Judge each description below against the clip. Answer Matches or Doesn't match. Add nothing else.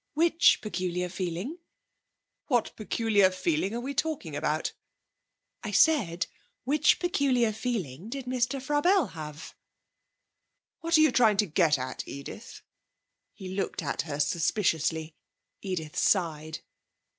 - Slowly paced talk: Matches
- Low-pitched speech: Doesn't match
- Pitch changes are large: Matches